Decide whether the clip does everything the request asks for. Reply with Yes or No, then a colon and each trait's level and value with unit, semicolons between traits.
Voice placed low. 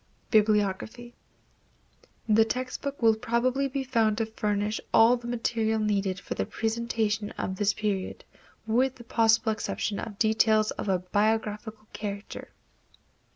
No: high, 220 Hz